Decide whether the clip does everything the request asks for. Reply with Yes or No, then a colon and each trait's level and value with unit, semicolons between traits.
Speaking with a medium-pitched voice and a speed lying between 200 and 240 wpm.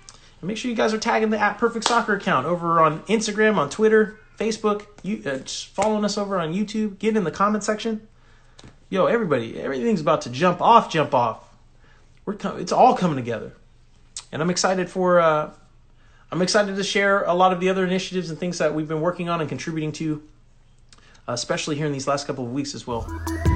Yes: medium, 180 Hz; fast, 205 wpm